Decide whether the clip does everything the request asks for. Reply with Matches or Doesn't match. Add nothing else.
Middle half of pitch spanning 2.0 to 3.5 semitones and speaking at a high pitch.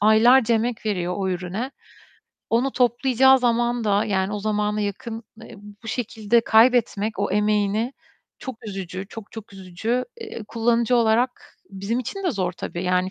Matches